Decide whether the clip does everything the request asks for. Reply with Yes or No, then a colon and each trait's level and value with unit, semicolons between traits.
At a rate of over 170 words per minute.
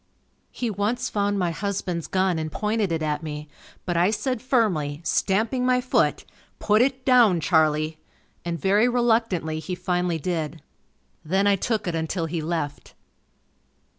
No: average, 150 wpm